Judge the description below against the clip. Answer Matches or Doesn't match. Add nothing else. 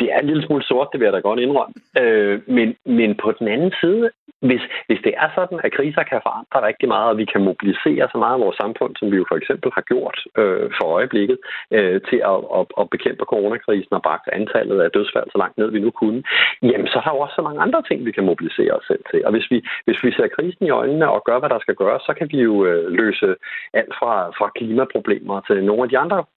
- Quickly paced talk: Matches